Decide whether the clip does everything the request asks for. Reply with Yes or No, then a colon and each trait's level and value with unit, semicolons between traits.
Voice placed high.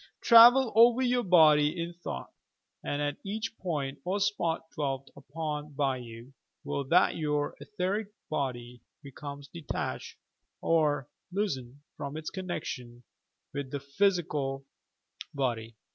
No: medium, 150 Hz